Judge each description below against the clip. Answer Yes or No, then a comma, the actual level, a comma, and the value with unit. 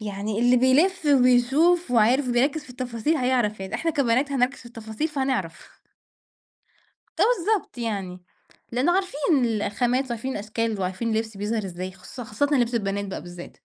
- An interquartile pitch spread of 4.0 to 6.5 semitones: Yes, average, 4.5 semitones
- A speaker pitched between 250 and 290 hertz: No, high, 240 Hz